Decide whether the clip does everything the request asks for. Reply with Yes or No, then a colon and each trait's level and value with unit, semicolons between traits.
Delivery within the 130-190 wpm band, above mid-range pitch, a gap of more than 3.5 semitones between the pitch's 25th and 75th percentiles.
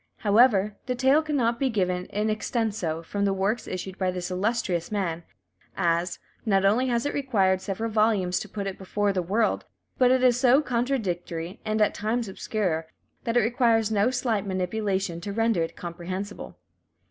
Yes: average, 170 wpm; high, 205 Hz; average, 4.0 semitones